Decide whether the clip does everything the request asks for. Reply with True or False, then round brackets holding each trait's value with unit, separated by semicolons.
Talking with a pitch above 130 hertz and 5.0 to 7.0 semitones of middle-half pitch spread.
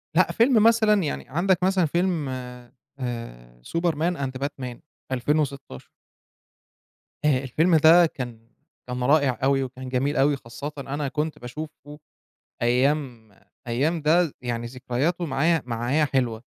False (140 Hz; 4.4 semitones)